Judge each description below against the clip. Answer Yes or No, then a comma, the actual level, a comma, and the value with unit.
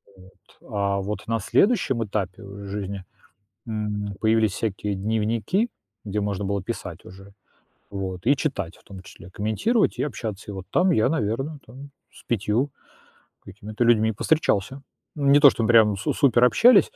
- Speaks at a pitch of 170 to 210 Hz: No, low, 110 Hz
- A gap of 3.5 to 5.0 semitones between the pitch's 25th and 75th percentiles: Yes, average, 4.2 semitones